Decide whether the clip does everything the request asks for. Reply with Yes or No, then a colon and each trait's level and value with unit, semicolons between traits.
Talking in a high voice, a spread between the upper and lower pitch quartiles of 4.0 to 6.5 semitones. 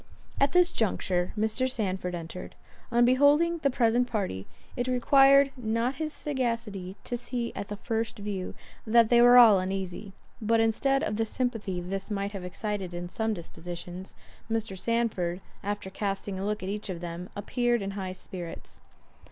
Yes: high, 215 Hz; average, 4.3 semitones